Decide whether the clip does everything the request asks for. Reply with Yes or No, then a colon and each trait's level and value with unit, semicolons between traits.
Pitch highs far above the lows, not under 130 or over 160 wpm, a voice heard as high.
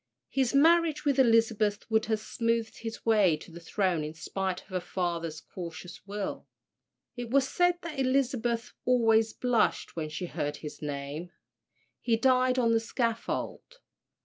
Yes: wide, 6.1 semitones; average, 150 wpm; high, 225 Hz